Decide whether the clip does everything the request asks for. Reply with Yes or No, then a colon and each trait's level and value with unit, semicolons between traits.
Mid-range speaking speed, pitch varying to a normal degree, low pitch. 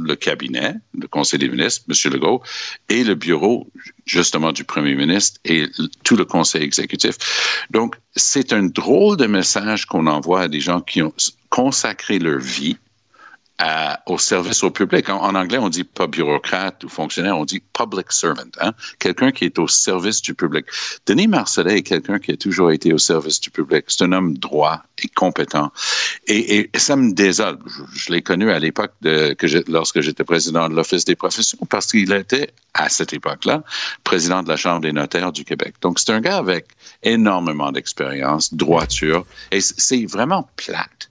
Yes: average, 185 wpm; average, 4.2 semitones; very low, 85 Hz